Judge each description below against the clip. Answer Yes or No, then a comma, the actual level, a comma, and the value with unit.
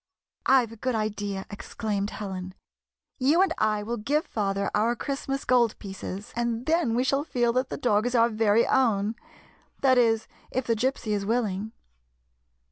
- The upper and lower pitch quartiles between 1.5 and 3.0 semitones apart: No, average, 3.5 semitones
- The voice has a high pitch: Yes, high, 230 Hz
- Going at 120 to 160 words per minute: No, average, 185 wpm